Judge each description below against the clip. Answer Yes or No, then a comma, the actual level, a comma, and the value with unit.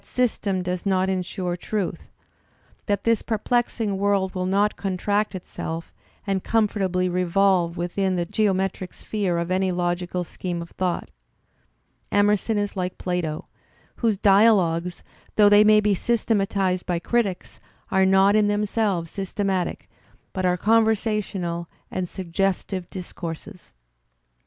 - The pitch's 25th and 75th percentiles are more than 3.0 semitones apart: No, narrow, 2.4 semitones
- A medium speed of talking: No, slow, 125 wpm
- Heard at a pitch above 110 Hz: Yes, high, 190 Hz